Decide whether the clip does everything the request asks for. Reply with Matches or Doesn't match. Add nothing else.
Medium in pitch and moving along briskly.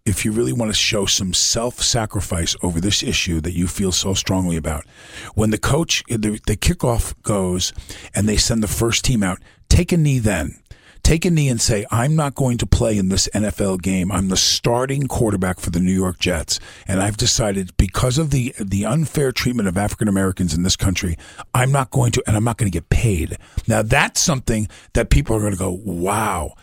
Doesn't match